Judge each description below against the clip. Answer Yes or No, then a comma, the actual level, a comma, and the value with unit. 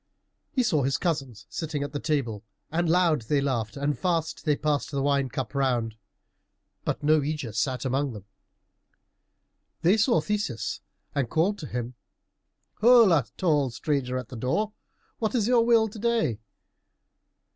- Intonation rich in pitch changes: Yes, wide, 5.9 semitones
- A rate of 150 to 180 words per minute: Yes, average, 155 wpm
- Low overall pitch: No, medium, 145 Hz